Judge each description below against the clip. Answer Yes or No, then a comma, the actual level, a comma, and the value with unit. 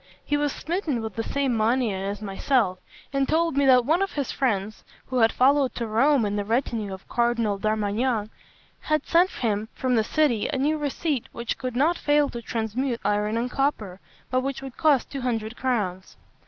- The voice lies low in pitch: No, high, 245 Hz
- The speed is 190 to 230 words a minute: Yes, average, 195 wpm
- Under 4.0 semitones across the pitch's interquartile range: No, average, 4.4 semitones